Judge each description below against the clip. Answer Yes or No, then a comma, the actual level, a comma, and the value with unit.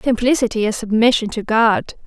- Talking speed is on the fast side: No, average, 145 wpm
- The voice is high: Yes, high, 225 Hz